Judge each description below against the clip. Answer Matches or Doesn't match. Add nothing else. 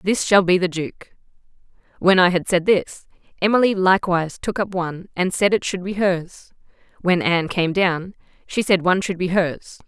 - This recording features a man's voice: Doesn't match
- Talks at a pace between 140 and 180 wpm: Doesn't match